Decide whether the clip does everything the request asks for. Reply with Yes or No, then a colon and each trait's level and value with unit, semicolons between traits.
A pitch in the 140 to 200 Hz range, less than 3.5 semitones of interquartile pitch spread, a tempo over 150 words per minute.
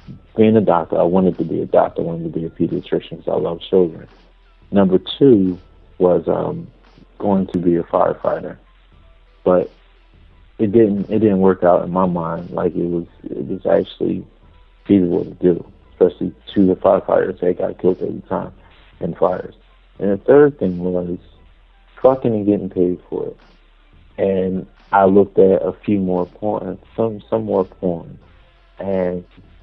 No: very low, 95 Hz; narrow, 2.5 semitones; average, 165 wpm